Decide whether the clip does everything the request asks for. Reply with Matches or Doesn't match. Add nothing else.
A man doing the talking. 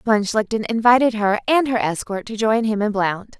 Doesn't match